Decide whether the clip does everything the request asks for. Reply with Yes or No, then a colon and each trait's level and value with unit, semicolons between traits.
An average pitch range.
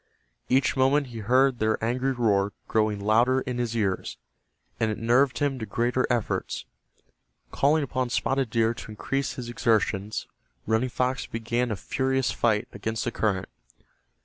Yes: average, 3.0 semitones